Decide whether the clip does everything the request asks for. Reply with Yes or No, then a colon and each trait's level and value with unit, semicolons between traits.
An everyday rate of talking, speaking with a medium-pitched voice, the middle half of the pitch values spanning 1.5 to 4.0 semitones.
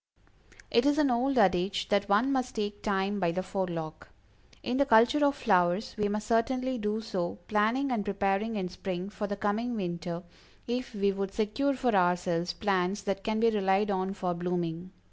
No: average, 185 wpm; high, 205 Hz; average, 3.7 semitones